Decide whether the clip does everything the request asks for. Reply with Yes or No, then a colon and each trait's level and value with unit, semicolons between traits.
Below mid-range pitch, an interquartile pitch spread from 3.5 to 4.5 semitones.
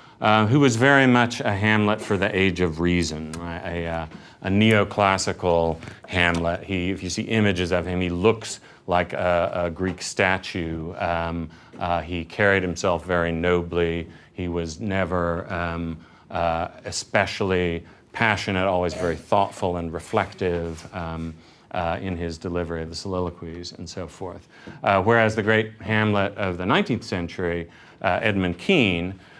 No: very low, 90 Hz; average, 2.8 semitones